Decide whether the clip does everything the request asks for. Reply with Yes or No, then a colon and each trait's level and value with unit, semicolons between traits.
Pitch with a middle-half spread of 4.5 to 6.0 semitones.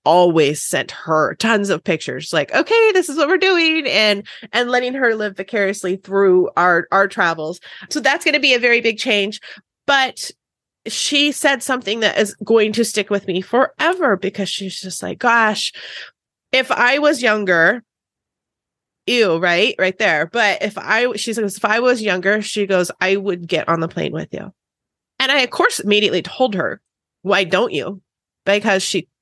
Yes: average, 4.8 semitones